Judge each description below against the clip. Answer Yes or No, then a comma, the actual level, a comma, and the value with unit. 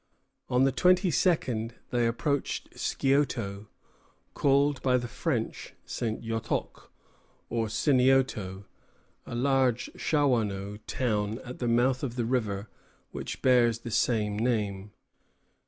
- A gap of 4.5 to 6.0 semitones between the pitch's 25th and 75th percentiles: No, average, 3.4 semitones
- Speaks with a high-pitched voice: No, low, 120 Hz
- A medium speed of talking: No, slow, 115 wpm